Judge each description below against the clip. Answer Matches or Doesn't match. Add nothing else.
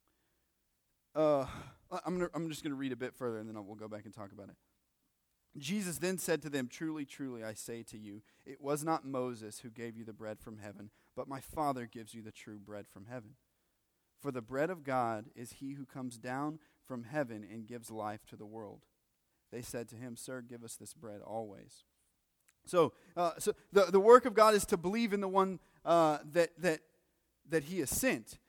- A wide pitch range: Matches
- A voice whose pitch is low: Matches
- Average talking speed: Doesn't match